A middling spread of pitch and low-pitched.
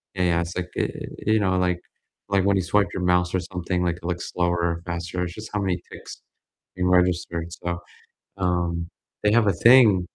No: narrow, 1.7 semitones; very low, 90 Hz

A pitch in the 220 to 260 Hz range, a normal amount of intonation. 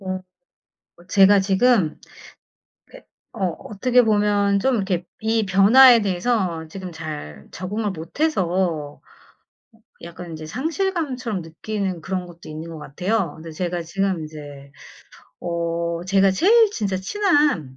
No: high, 190 Hz; average, 4.7 semitones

